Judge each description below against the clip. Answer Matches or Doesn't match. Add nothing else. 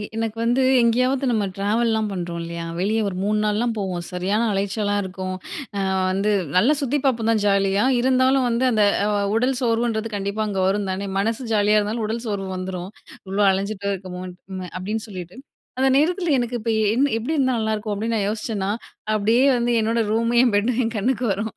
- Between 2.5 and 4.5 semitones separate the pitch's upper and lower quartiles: Matches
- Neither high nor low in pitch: Doesn't match